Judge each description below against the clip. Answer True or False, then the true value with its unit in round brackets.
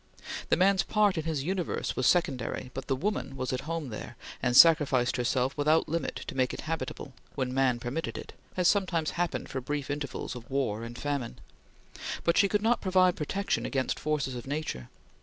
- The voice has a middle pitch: True (145 Hz)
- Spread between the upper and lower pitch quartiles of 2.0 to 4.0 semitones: False (4.7 semitones)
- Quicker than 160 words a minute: True (190 wpm)